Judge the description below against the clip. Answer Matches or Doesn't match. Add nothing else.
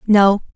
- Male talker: Doesn't match